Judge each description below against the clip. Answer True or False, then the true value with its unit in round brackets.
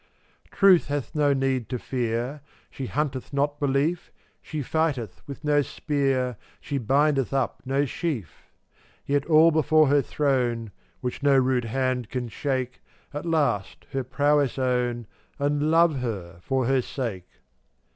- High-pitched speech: False (135 Hz)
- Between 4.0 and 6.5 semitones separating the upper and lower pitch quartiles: False (2.8 semitones)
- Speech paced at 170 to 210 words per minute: False (145 wpm)